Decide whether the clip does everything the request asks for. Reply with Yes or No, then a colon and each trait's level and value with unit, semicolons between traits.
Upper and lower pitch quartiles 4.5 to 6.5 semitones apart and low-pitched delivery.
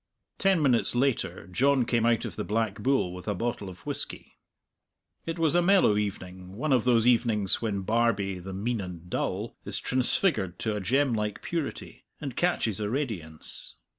Yes: average, 5.3 semitones; low, 115 Hz